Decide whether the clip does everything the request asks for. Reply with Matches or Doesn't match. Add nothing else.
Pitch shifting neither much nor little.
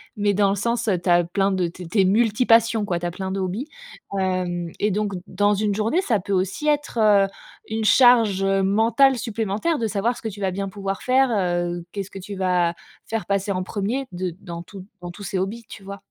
Matches